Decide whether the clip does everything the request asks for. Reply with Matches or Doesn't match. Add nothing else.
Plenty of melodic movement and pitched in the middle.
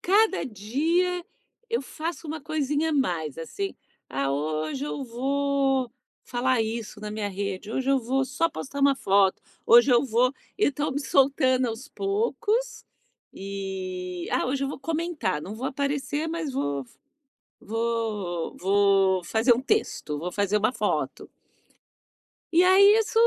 Doesn't match